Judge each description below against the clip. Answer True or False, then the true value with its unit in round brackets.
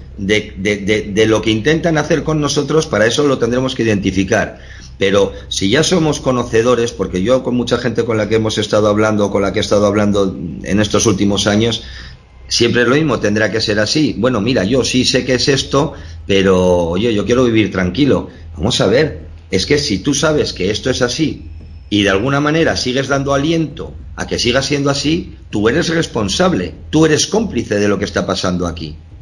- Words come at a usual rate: False (205 wpm)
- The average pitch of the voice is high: False (110 Hz)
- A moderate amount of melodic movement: False (6.0 semitones)